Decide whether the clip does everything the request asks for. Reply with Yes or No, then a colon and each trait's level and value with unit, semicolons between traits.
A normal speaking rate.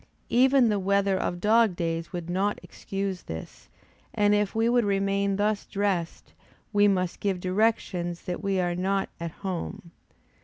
Yes: average, 155 wpm